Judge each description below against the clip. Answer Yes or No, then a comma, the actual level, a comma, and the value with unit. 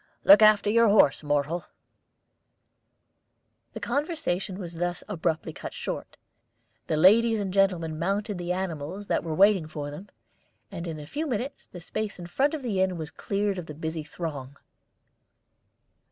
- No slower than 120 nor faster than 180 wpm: Yes, average, 155 wpm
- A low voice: No, medium, 180 Hz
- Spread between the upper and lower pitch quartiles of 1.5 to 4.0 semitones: No, average, 4.5 semitones